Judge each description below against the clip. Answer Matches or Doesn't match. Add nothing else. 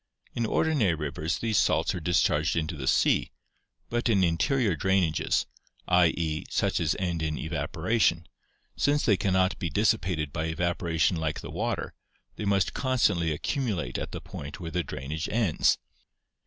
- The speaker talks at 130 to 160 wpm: Matches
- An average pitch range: Matches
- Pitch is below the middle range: Matches